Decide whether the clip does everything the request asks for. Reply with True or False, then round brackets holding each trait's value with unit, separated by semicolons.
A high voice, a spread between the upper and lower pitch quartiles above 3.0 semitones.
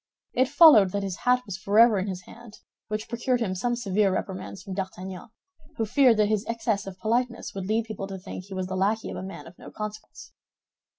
True (210 Hz; 3.4 semitones)